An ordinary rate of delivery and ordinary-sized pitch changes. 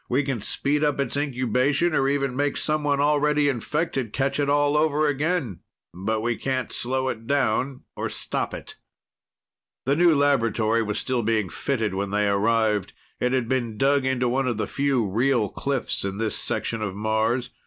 Yes: average, 175 wpm; average, 4.2 semitones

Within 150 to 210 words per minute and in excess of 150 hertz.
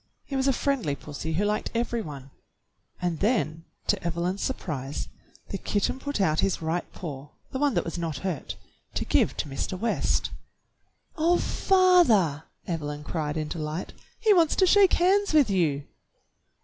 Yes: average, 160 wpm; medium, 185 Hz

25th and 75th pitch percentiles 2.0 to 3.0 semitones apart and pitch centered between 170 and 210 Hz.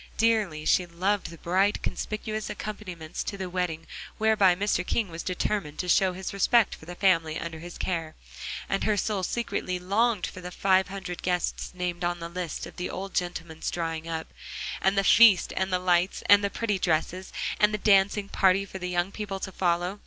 Yes: narrow, 2.5 semitones; medium, 185 Hz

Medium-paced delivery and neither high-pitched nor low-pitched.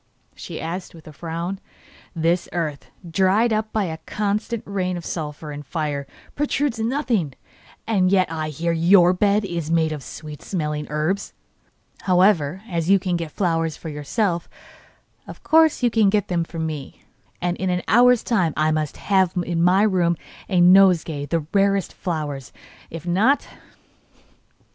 Yes: average, 160 wpm; medium, 175 Hz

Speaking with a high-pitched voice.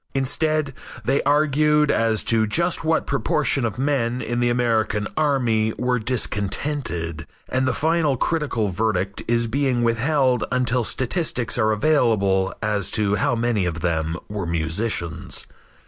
No: low, 120 Hz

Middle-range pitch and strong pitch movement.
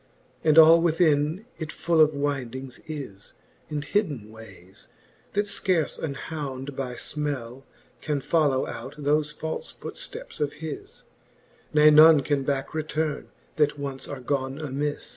No: medium, 145 Hz; average, 2.7 semitones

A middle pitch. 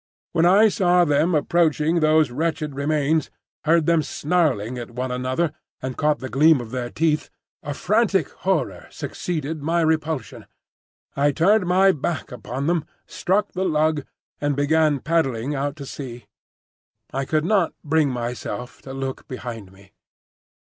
Yes: medium, 150 Hz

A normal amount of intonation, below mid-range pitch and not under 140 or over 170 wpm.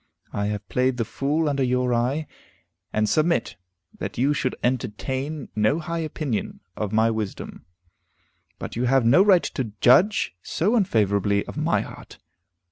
No: wide, 5.9 semitones; low, 125 Hz; average, 150 wpm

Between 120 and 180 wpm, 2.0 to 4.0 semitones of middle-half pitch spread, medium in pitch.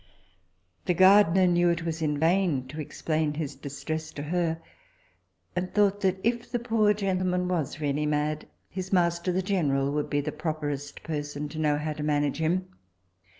Yes: average, 170 wpm; average, 3.6 semitones; medium, 160 Hz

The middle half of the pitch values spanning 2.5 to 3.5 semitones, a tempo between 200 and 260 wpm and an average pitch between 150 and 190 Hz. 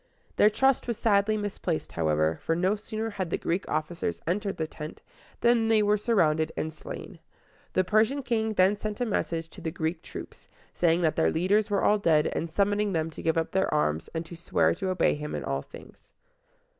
No: average, 4.6 semitones; fast, 205 wpm; medium, 185 Hz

